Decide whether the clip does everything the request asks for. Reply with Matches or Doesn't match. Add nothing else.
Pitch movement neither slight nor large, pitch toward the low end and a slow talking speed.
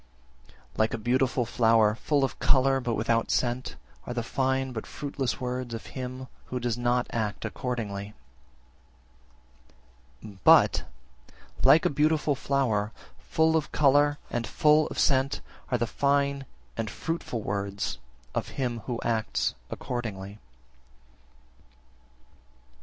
Matches